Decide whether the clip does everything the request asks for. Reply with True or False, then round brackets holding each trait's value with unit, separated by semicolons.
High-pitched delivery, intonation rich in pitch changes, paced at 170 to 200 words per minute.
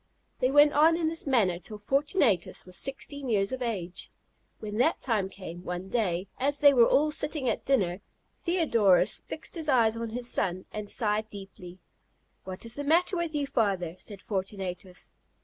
True (225 Hz; 6.8 semitones; 175 wpm)